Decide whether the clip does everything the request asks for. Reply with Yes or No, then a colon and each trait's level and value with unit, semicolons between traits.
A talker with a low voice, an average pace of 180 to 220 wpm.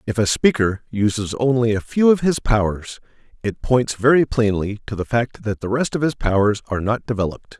Yes: low, 115 Hz; fast, 205 wpm